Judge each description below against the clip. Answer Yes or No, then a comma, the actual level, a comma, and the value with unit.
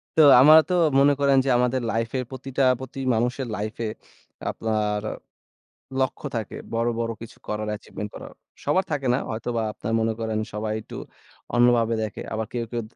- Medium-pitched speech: No, low, 115 Hz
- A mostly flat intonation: No, average, 3.1 semitones